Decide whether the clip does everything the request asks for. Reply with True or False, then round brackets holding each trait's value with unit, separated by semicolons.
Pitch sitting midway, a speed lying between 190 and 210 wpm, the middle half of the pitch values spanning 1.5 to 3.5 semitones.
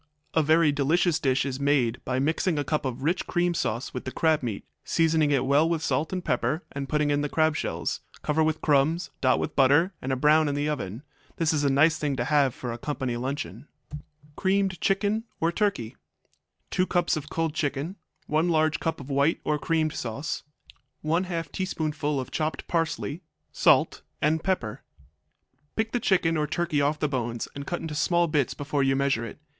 True (150 Hz; 195 wpm; 3.0 semitones)